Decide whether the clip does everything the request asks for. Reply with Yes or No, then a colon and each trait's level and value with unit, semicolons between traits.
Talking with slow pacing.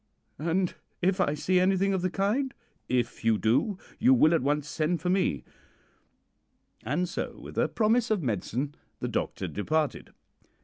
No: average, 160 wpm